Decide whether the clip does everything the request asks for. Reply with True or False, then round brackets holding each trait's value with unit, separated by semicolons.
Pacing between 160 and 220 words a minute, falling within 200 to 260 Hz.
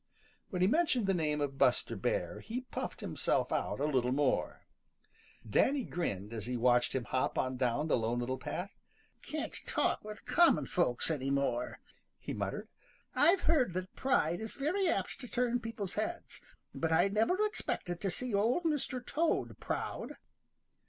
False (165 wpm; 185 Hz)